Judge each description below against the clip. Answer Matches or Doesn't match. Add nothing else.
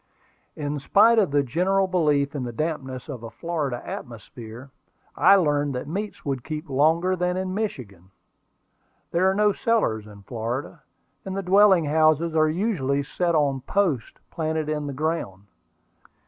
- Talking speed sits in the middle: Matches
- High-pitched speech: Doesn't match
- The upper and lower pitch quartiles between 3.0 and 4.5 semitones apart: Doesn't match